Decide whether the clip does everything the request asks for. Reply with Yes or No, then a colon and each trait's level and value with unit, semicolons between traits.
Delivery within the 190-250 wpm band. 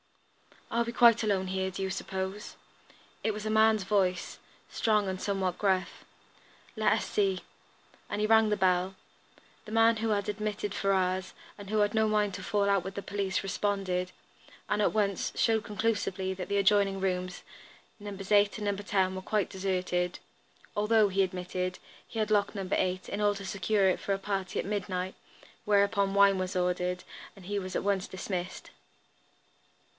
No: average, 175 wpm